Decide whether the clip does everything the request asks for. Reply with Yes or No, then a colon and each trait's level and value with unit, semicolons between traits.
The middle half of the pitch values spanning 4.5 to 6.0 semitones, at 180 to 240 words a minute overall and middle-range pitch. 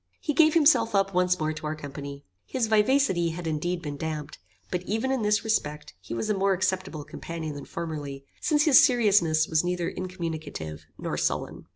Yes: wide, 5.5 semitones; average, 185 wpm; medium, 175 Hz